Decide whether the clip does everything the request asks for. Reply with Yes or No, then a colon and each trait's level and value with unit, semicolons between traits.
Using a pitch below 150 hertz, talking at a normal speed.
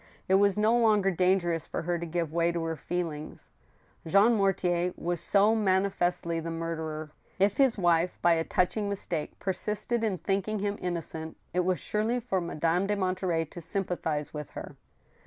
No: medium, 180 Hz; average, 170 wpm